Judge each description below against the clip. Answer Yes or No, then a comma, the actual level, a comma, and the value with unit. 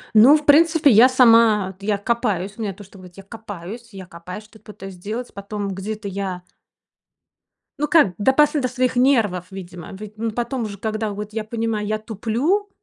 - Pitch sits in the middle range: No, high, 215 Hz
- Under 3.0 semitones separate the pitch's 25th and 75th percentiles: No, average, 3.4 semitones